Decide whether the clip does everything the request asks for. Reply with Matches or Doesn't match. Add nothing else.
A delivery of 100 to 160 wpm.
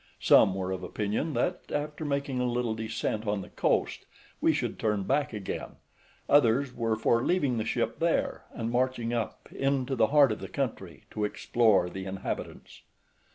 Doesn't match